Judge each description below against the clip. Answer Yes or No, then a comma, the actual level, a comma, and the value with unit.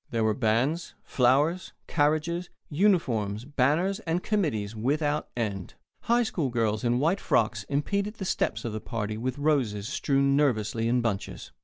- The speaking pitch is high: No, low, 135 Hz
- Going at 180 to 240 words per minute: No, average, 150 wpm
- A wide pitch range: Yes, wide, 6.4 semitones